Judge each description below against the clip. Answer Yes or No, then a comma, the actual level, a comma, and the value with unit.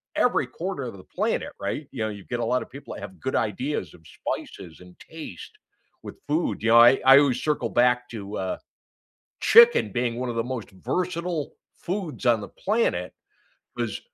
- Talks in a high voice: No, low, 125 Hz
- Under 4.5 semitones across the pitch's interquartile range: No, wide, 5.6 semitones